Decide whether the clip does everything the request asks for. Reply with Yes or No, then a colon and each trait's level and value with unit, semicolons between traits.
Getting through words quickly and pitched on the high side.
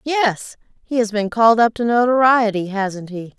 No: average, 175 wpm; high, 225 Hz